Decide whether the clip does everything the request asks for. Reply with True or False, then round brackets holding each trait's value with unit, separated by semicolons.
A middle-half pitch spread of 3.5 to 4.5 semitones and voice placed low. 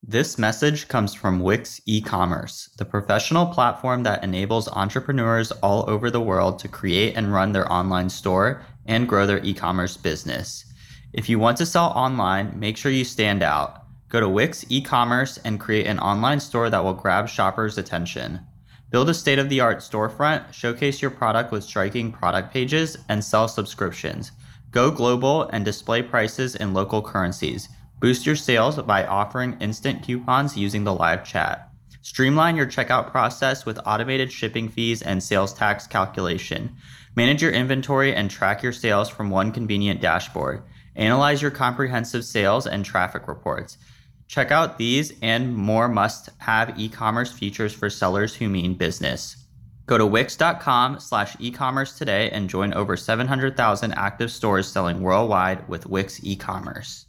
True (4.1 semitones; 115 Hz)